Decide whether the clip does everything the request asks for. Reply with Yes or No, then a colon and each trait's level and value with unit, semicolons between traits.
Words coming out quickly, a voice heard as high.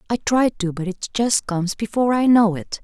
Yes: fast, 235 wpm; high, 210 Hz